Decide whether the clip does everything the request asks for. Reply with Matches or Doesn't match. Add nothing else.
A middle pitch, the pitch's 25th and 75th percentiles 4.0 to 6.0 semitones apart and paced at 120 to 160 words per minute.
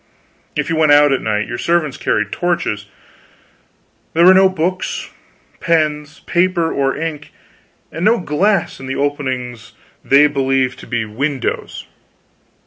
Matches